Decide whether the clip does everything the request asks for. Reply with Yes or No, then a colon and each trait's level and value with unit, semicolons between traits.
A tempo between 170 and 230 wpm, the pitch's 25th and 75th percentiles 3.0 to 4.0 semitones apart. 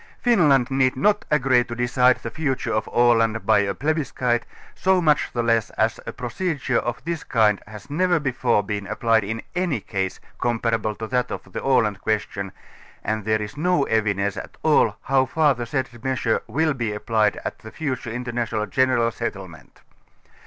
Yes: average, 175 wpm; average, 3.7 semitones